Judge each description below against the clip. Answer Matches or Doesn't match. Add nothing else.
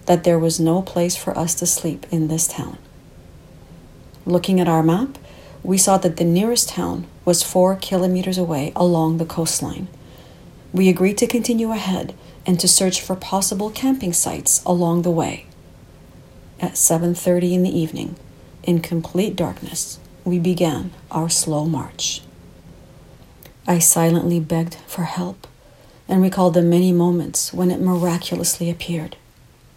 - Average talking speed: Matches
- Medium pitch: Matches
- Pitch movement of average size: Doesn't match